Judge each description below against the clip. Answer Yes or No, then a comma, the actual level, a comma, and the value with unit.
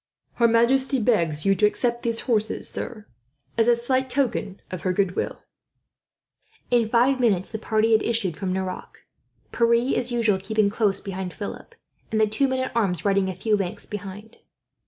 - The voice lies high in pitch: Yes, high, 220 Hz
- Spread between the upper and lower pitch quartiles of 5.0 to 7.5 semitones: No, average, 3.4 semitones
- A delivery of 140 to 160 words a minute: No, average, 175 wpm